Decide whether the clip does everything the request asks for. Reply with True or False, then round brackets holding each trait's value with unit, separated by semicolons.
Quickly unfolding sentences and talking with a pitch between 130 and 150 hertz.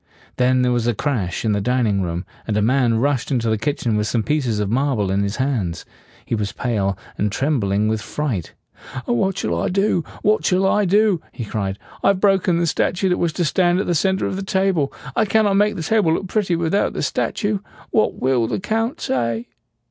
True (215 wpm; 135 Hz)